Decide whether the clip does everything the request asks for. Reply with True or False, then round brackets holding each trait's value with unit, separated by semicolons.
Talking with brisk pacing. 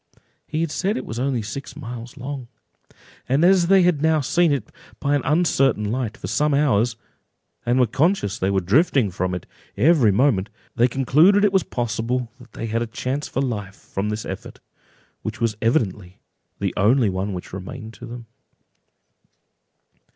False (175 wpm)